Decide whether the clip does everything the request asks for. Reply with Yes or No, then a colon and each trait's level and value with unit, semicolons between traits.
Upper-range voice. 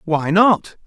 No: medium, 180 Hz